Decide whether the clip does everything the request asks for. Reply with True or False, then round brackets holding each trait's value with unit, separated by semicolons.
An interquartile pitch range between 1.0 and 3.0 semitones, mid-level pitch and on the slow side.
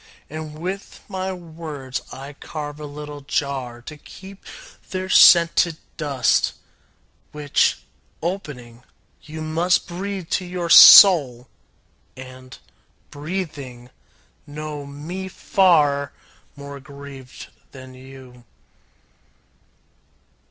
False (4.2 semitones; 150 Hz; 90 wpm)